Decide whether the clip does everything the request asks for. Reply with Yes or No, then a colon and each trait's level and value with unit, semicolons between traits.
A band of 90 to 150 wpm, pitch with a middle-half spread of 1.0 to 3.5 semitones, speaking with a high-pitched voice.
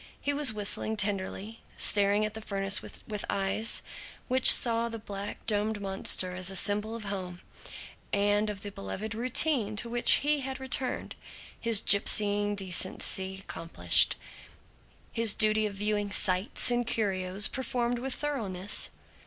Yes: average, 140 wpm; average, 2.8 semitones; high, 210 Hz